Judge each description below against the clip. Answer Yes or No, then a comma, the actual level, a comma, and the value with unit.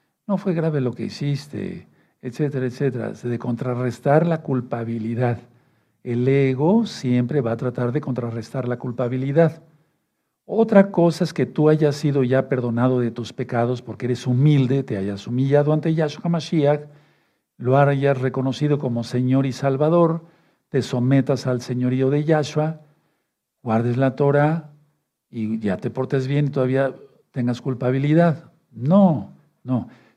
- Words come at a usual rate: Yes, average, 140 wpm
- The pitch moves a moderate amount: Yes, average, 3.4 semitones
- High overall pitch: No, low, 135 Hz